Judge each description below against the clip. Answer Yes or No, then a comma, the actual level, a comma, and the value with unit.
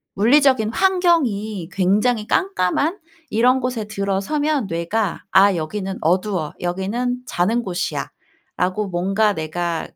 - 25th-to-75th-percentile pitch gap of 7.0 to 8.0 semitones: No, average, 5.3 semitones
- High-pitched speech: Yes, high, 205 Hz